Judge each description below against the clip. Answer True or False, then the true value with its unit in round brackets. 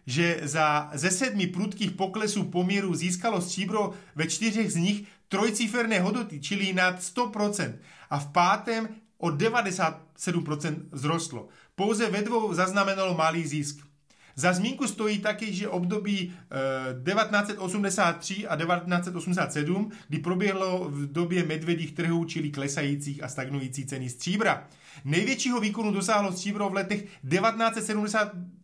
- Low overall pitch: False (185 Hz)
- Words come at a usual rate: True (120 wpm)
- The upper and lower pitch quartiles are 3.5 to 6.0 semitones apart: True (4.3 semitones)